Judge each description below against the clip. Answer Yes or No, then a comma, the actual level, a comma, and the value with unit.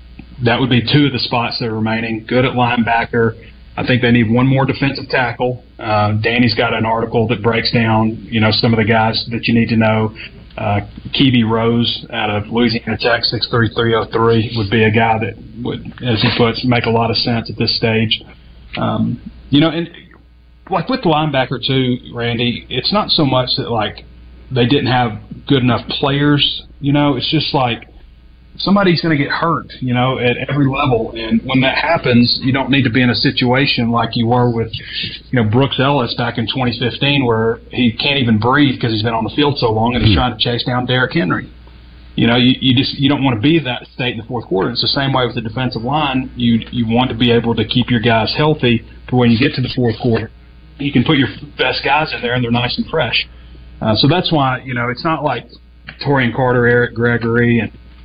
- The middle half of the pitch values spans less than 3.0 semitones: Yes, narrow, 2.6 semitones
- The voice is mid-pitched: No, low, 120 Hz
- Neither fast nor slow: No, fast, 230 wpm